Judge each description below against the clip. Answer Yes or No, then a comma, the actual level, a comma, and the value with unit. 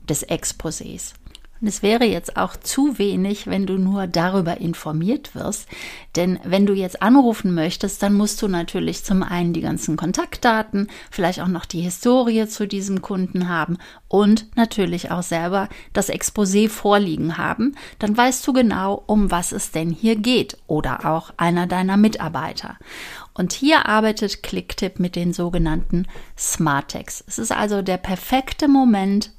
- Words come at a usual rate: Yes, average, 155 wpm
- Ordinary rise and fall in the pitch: Yes, average, 3.7 semitones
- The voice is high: Yes, high, 195 Hz